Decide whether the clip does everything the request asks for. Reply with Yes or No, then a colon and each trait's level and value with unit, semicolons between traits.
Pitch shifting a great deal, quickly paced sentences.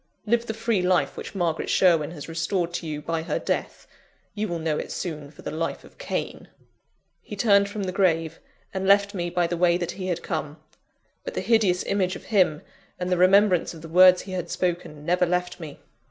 No: average, 2.9 semitones; fast, 210 wpm